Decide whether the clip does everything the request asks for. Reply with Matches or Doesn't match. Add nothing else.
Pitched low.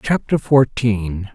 Matches